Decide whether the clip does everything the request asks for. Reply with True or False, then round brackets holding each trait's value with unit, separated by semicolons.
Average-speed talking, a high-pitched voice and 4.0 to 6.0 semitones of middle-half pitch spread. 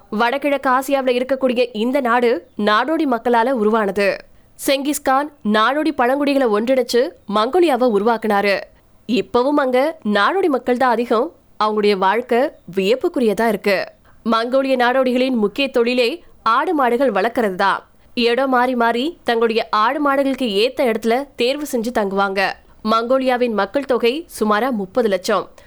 False (95 wpm; 245 Hz; 3.5 semitones)